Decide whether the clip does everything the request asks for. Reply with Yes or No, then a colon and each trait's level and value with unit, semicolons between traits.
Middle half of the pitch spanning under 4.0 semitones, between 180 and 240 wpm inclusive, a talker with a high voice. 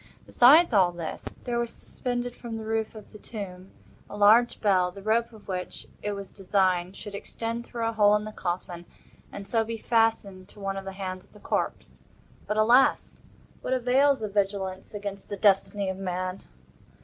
Yes: average, 2.9 semitones; average, 185 wpm; high, 205 Hz